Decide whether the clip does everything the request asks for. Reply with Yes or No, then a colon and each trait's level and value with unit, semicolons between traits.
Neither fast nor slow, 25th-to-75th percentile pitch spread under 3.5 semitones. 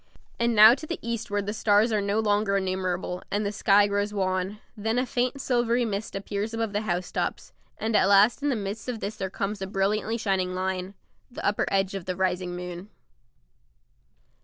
Yes: average, 190 wpm; narrow, 2.6 semitones